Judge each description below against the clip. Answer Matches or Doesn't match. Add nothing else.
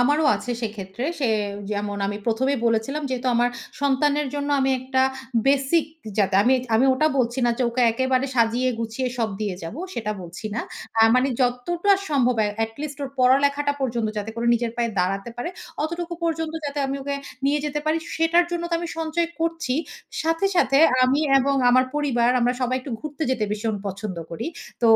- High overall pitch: Matches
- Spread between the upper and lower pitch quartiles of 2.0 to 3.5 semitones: Doesn't match